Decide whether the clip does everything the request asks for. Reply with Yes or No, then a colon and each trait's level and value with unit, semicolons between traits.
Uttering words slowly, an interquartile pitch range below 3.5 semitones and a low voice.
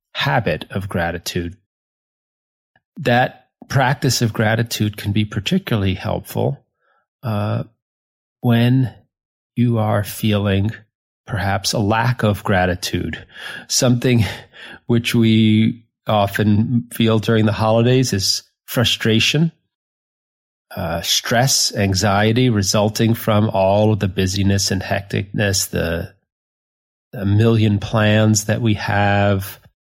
Yes: slow, 100 wpm; average, 2.8 semitones; low, 110 Hz